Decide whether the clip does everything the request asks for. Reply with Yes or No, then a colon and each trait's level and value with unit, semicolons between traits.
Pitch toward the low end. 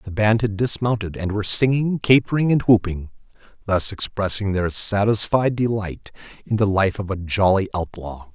Yes: low, 105 Hz